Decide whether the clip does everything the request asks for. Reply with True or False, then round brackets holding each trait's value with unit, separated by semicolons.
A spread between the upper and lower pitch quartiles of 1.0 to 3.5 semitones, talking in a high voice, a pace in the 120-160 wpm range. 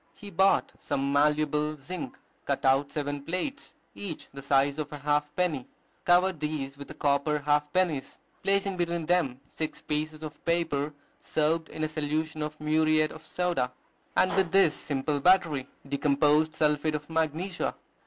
False (2.6 semitones; 155 Hz; 155 wpm)